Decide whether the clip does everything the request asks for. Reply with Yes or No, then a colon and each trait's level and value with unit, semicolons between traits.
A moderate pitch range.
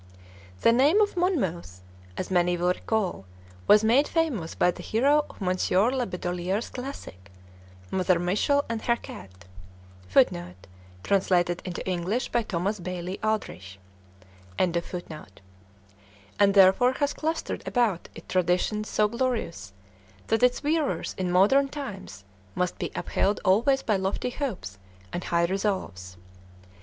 No: wide, 5.7 semitones